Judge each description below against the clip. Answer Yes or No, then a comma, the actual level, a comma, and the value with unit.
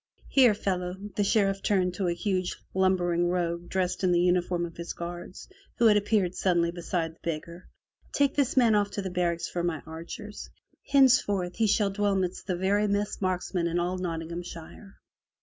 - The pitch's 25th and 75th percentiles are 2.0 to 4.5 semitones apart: Yes, average, 2.8 semitones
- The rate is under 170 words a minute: No, average, 185 wpm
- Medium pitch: Yes, medium, 180 Hz